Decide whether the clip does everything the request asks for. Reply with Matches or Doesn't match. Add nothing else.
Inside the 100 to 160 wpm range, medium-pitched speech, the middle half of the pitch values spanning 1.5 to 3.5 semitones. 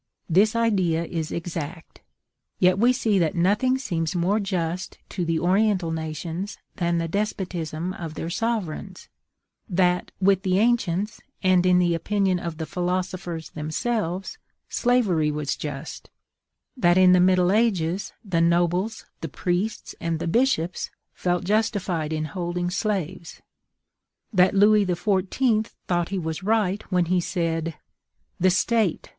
Matches